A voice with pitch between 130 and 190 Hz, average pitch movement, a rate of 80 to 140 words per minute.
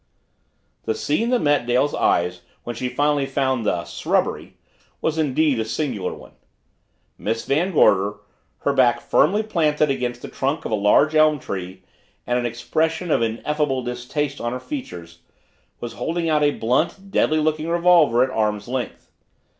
No: low, 135 Hz; average, 4.9 semitones; average, 160 wpm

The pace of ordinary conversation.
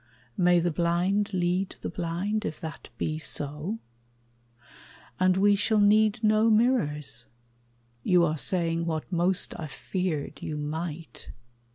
No: slow, 130 wpm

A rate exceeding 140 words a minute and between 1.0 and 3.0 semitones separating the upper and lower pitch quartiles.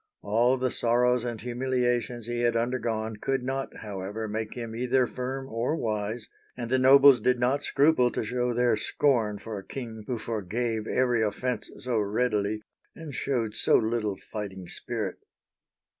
Yes: average, 160 wpm; narrow, 2.5 semitones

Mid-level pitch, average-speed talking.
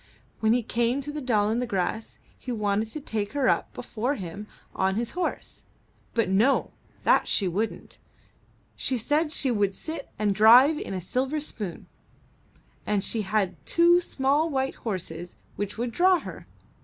No: high, 230 Hz; average, 170 wpm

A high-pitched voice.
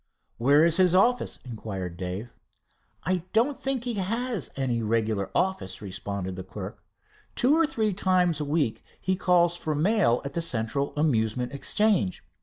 No: medium, 150 Hz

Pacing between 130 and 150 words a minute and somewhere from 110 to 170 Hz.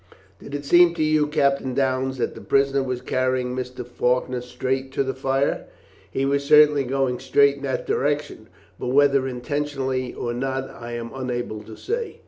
No: average, 175 wpm; low, 135 Hz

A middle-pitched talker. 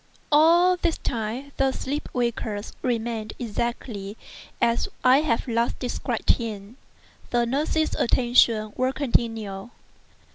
No: high, 240 Hz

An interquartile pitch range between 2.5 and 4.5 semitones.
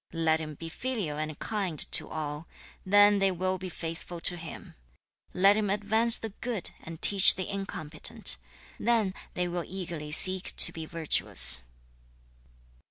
Yes: average, 4.0 semitones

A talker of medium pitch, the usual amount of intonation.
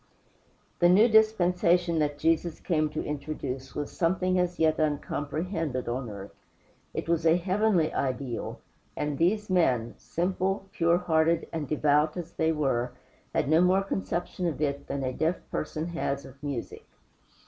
Yes: medium, 160 Hz; average, 3.6 semitones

